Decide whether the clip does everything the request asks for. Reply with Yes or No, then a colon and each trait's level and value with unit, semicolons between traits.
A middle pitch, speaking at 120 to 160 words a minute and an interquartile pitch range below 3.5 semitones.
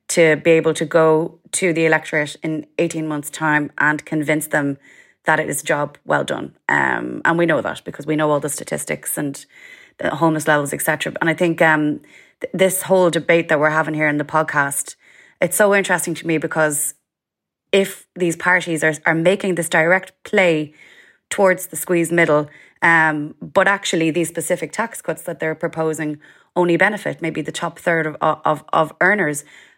No: medium, 160 Hz; average, 185 wpm; narrow, 2.5 semitones